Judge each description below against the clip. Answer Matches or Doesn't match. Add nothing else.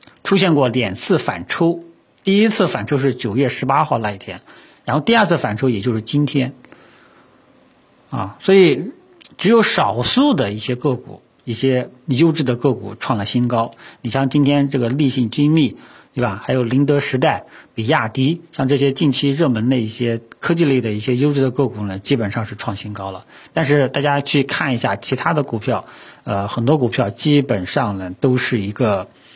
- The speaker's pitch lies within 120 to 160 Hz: Matches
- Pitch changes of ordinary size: Matches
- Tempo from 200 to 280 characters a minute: Matches